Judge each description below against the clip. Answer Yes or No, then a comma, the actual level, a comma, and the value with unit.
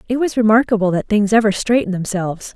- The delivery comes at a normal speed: Yes, average, 190 wpm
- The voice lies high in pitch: Yes, high, 210 Hz